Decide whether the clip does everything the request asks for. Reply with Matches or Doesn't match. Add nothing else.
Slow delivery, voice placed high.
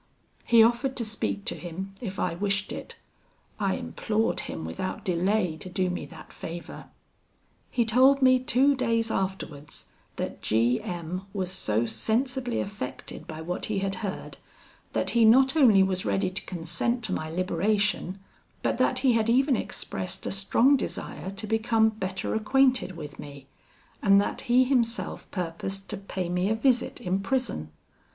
Doesn't match